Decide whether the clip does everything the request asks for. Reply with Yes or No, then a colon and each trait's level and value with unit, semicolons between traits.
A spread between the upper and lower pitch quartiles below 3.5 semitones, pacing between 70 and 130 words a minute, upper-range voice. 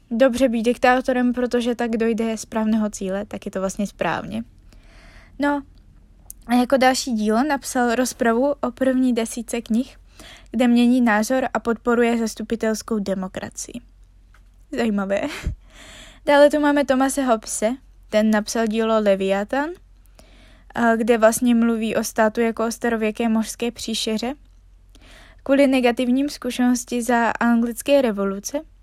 Yes: narrow, 2.4 semitones; average, 120 wpm; high, 235 Hz